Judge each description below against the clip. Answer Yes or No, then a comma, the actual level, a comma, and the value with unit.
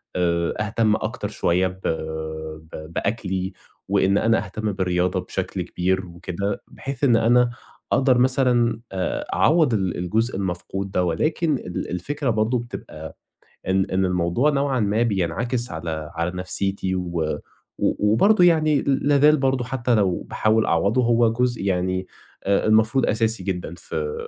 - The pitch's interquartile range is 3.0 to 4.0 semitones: No, average, 5.0 semitones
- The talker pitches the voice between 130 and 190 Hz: No, low, 105 Hz